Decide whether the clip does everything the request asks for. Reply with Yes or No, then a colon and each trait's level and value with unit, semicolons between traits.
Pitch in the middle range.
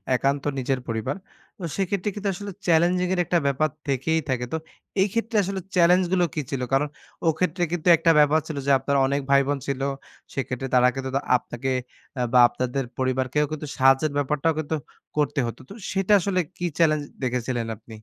Yes: medium, 145 Hz